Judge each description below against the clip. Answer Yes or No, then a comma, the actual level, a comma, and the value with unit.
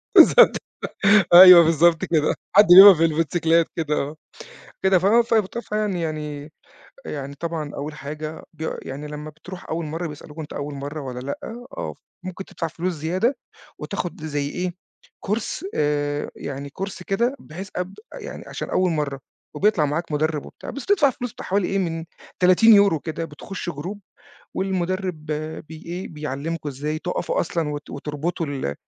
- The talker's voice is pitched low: No, medium, 165 Hz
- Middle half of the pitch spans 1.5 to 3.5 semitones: No, average, 3.9 semitones